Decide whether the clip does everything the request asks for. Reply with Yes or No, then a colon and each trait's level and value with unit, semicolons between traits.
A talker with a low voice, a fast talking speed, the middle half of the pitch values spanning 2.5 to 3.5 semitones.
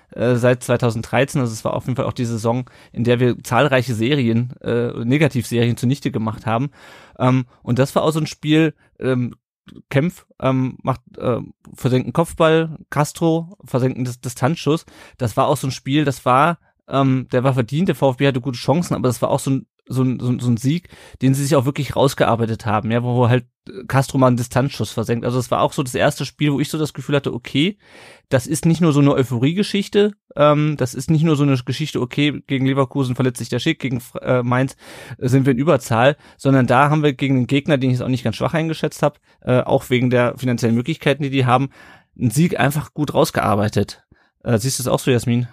Yes: low, 130 Hz; fast, 220 wpm; average, 3.1 semitones